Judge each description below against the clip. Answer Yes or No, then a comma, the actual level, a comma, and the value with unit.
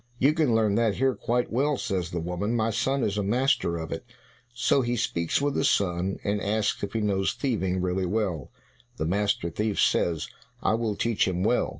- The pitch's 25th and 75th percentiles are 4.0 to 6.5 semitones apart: Yes, average, 4.3 semitones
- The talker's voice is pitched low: Yes, low, 105 Hz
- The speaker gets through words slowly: No, fast, 205 wpm